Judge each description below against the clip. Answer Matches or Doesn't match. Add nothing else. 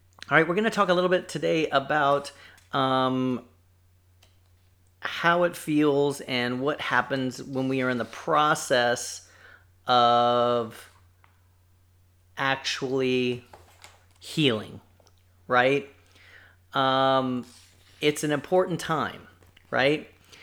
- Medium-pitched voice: Doesn't match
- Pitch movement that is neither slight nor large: Doesn't match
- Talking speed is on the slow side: Matches